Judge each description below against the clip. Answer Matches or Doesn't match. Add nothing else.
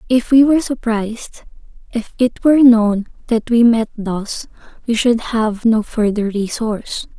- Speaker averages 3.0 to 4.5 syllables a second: Matches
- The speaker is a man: Doesn't match